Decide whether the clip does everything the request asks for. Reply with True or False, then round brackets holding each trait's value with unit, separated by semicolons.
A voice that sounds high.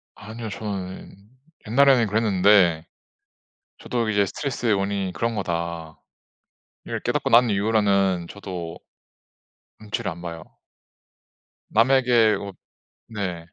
False (100 Hz)